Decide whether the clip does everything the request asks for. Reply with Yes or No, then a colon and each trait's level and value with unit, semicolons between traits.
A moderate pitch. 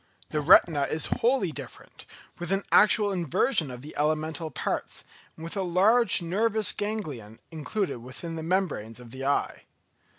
Yes: medium, 165 Hz